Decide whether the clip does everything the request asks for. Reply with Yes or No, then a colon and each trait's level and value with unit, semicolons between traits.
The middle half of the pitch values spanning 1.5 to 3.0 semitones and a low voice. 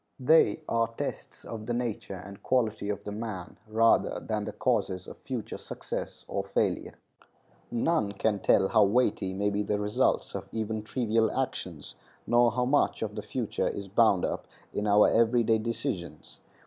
Yes: narrow, 2.5 semitones; low, 110 Hz